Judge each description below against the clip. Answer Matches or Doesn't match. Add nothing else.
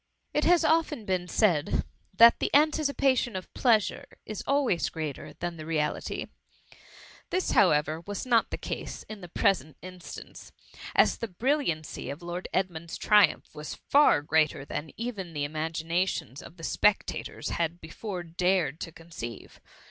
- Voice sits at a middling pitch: Matches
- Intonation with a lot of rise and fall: Matches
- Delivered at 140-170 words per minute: Matches